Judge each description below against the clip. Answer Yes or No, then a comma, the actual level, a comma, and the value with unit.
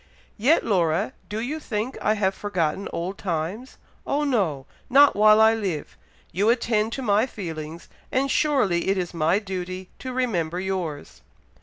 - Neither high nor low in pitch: No, high, 200 Hz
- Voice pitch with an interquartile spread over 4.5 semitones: Yes, average, 5.1 semitones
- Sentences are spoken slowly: No, average, 155 wpm